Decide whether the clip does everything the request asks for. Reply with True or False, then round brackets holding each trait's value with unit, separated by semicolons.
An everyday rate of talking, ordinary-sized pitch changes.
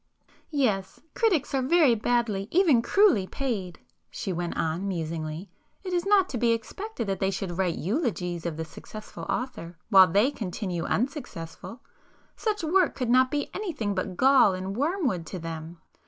False (145 wpm; 7.7 semitones)